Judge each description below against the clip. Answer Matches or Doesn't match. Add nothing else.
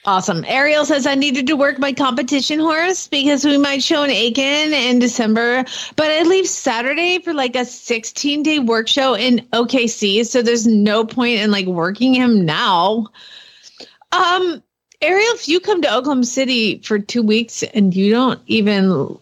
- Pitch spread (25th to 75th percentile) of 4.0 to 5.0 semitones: Matches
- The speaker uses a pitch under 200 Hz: Doesn't match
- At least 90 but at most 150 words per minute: Doesn't match